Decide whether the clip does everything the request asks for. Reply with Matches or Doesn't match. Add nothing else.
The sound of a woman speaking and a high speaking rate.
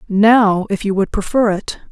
Doesn't match